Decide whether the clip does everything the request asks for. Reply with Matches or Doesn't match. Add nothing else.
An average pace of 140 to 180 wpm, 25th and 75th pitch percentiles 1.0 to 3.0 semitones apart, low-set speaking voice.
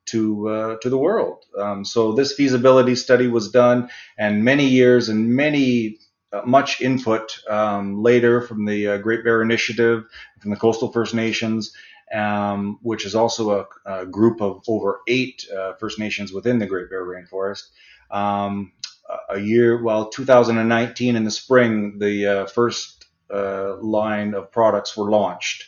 Matches